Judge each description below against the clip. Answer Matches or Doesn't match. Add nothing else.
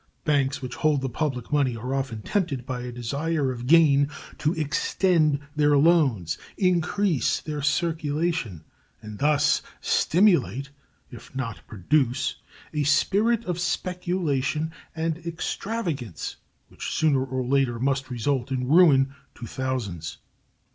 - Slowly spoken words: Matches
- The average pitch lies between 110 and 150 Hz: Matches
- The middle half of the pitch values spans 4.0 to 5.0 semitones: Matches